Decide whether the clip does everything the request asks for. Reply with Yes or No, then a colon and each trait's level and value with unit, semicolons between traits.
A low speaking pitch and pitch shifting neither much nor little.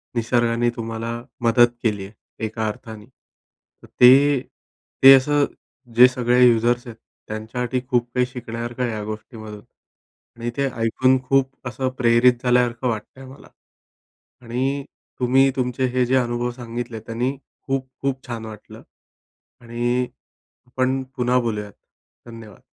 No: low, 120 Hz; narrow, 1.9 semitones